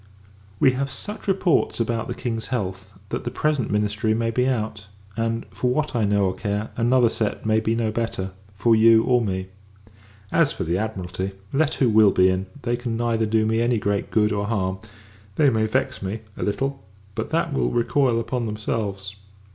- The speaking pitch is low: Yes, low, 110 Hz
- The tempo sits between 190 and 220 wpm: Yes, average, 195 wpm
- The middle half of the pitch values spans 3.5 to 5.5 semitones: No, average, 2.8 semitones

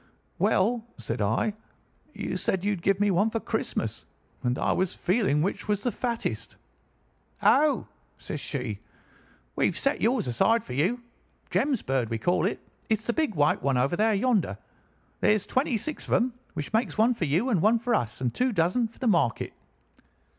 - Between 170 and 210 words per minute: Yes, average, 175 wpm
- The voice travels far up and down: Yes, wide, 6.8 semitones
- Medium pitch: No, high, 205 Hz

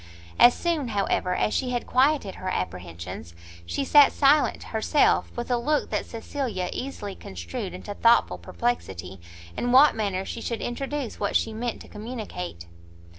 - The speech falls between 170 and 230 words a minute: No, average, 155 wpm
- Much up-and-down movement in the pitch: Yes, wide, 6.1 semitones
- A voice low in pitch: No, high, 230 Hz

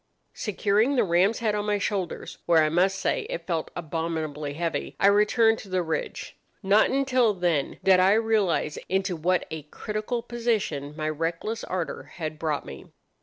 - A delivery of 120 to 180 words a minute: Yes, average, 170 wpm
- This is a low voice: No, medium, 185 Hz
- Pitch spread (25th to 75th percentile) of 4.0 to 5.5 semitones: Yes, average, 4.7 semitones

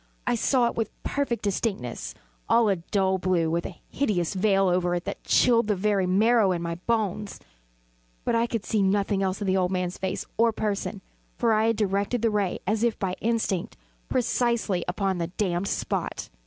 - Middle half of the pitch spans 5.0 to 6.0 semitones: No, average, 3.5 semitones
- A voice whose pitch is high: Yes, high, 200 Hz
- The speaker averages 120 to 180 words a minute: No, average, 190 wpm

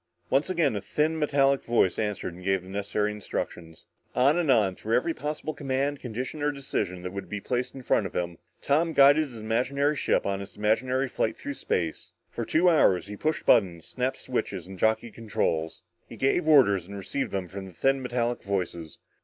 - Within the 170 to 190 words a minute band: No, average, 200 wpm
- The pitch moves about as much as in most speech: No, wide, 6.1 semitones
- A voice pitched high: No, low, 115 Hz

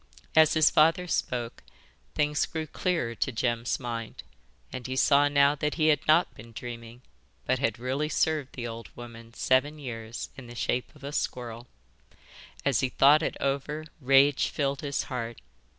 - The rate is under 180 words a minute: Yes, average, 165 wpm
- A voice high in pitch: No, low, 135 Hz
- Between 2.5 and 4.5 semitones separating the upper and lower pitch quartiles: Yes, average, 3.9 semitones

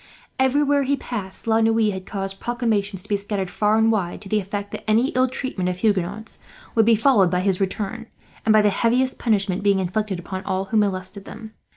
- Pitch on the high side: Yes, high, 210 Hz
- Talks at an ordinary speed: No, fast, 210 wpm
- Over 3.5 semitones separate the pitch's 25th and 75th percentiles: No, average, 2.8 semitones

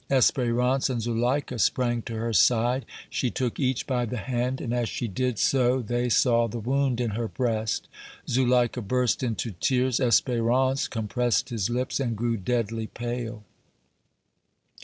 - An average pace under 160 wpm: Yes, average, 150 wpm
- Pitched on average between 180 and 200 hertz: No, low, 120 Hz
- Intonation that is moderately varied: No, narrow, 1.7 semitones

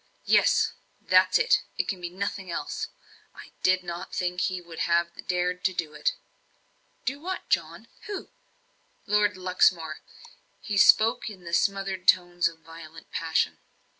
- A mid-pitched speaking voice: Yes, medium, 180 Hz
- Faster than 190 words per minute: No, average, 145 wpm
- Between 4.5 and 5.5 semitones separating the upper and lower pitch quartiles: No, narrow, 2.6 semitones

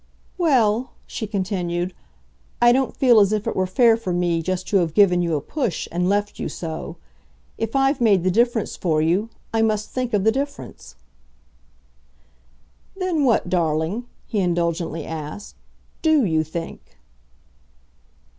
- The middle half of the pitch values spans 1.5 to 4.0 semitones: No, wide, 5.4 semitones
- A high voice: Yes, high, 200 Hz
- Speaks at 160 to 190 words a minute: No, average, 150 wpm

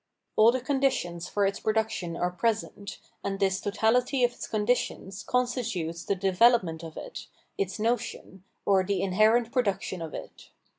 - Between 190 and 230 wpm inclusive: No, average, 160 wpm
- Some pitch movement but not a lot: Yes, average, 4.2 semitones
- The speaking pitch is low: No, high, 205 Hz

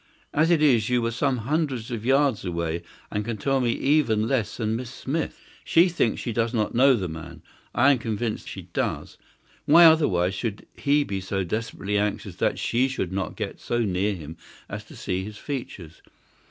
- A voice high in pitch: No, low, 115 Hz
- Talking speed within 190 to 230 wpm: Yes, average, 195 wpm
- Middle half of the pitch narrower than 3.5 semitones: No, average, 5.2 semitones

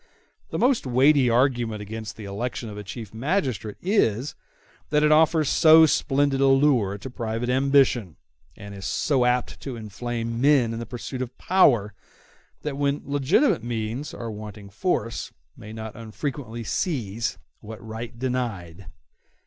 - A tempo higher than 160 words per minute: No, average, 150 wpm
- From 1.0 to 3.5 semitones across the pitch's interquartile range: No, average, 4.1 semitones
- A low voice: Yes, low, 120 Hz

